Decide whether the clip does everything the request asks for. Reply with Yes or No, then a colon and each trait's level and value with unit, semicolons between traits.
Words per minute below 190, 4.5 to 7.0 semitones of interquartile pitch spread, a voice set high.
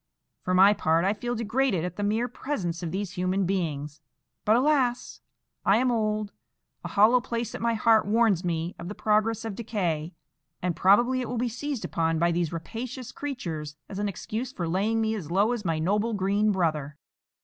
No: average, 195 wpm; average, 5.0 semitones; high, 205 Hz